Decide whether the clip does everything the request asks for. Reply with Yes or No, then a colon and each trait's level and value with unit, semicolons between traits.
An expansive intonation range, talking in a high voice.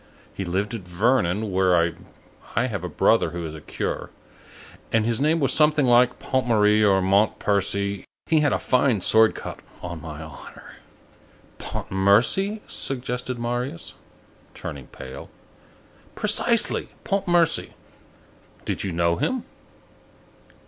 No: wide, 6.0 semitones; low, 105 Hz